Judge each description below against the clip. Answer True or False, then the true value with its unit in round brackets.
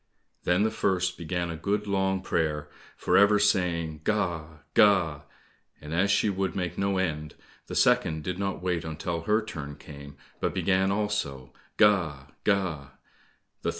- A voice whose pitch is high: False (90 Hz)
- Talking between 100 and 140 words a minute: False (150 wpm)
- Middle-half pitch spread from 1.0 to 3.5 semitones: False (4.1 semitones)